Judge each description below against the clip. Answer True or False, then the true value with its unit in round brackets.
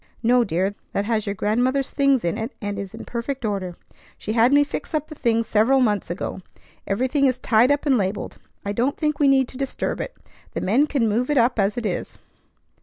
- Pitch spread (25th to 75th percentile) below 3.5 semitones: False (4.7 semitones)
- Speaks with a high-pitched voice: True (235 Hz)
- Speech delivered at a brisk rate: True (220 wpm)